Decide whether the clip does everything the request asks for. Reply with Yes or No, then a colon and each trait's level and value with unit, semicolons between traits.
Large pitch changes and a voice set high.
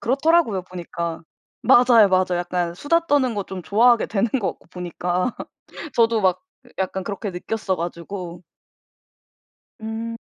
No: average, 4.4 semitones; high, 195 Hz